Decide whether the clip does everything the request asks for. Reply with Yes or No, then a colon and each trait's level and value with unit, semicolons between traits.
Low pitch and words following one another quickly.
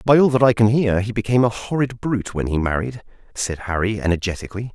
Yes: low, 110 Hz; fast, 215 wpm